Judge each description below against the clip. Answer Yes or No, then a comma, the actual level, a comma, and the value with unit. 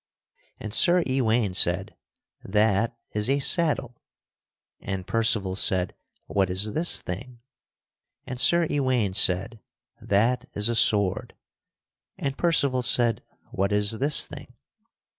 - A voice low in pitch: Yes, low, 115 Hz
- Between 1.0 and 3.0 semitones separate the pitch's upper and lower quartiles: No, average, 4.6 semitones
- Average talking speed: No, slow, 120 wpm